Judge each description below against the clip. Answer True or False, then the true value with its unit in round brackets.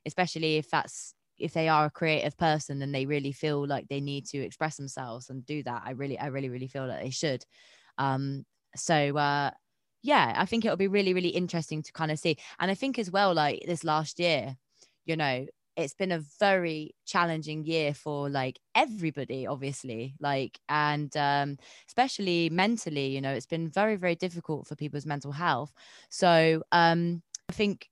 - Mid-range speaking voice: True (150 Hz)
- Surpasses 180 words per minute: True (190 wpm)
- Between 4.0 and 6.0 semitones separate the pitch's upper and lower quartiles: False (3.5 semitones)